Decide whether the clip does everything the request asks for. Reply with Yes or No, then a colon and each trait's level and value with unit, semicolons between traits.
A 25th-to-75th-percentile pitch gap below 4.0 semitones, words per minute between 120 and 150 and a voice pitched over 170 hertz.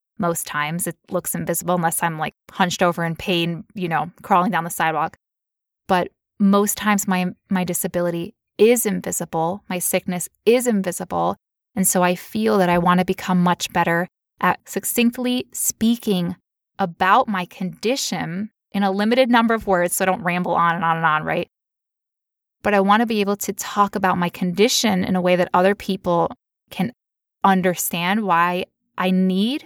No: average, 2.8 semitones; average, 170 wpm; medium, 185 Hz